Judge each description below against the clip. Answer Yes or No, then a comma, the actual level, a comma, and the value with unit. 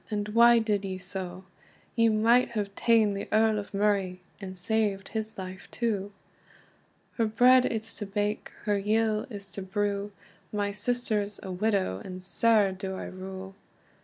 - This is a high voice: Yes, high, 205 Hz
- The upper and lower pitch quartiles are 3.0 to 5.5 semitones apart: No, narrow, 2.4 semitones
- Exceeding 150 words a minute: Yes, average, 160 wpm